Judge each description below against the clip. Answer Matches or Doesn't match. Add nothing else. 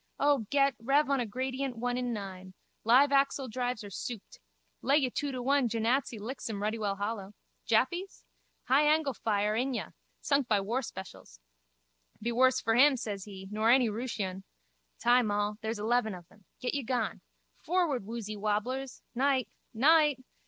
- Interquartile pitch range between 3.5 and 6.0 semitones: Matches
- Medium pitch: Doesn't match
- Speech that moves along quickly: Doesn't match